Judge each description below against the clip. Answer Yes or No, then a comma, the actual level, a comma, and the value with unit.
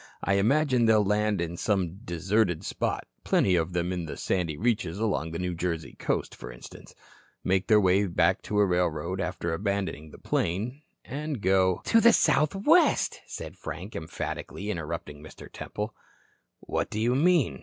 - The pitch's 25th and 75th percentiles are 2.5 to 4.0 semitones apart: No, average, 4.4 semitones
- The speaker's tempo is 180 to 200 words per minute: No, average, 165 wpm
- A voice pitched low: Yes, very low, 95 Hz